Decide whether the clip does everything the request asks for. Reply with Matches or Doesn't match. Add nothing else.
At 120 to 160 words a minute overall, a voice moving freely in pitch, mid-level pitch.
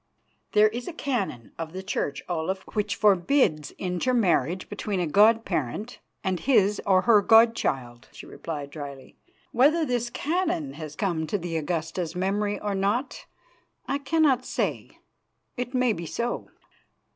Doesn't match